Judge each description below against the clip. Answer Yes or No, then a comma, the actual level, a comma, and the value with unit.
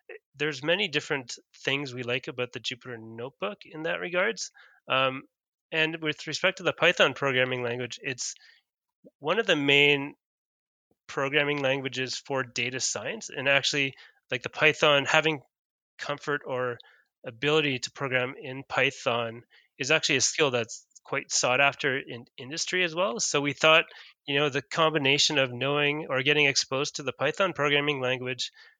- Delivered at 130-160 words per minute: Yes, average, 155 wpm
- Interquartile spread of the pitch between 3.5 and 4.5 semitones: No, average, 3.0 semitones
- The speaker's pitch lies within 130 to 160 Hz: Yes, medium, 140 Hz